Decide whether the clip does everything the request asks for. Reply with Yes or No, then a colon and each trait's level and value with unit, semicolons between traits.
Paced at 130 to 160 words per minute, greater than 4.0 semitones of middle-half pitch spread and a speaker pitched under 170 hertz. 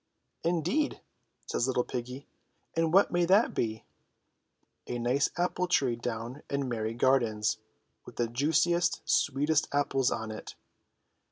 Yes: slow, 135 wpm; wide, 5.6 semitones; low, 135 Hz